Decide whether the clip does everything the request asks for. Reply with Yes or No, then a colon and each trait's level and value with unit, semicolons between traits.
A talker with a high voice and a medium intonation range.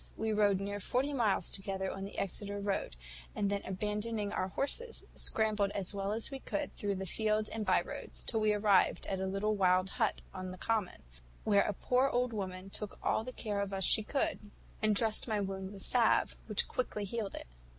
No: high, 205 Hz; narrow, 2.1 semitones